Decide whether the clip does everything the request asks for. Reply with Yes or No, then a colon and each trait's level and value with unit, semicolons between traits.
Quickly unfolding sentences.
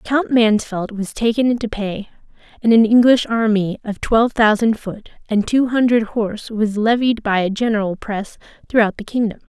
No: average, 170 wpm